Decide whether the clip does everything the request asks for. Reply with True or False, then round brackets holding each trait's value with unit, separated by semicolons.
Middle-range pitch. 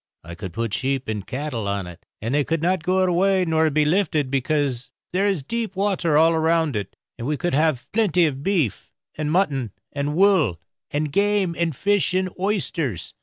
True (155 Hz)